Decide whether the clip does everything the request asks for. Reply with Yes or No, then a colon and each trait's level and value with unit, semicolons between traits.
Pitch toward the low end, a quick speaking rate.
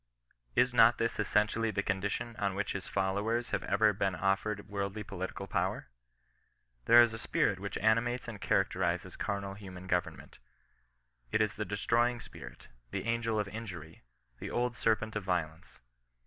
No: low, 100 Hz; average, 160 wpm